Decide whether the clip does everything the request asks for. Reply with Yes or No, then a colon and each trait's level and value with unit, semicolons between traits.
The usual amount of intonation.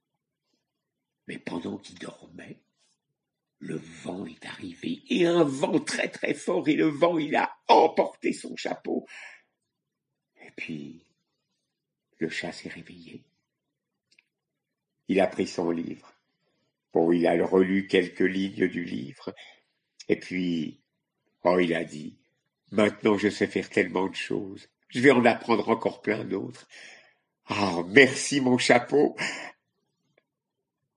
No: wide, 7.4 semitones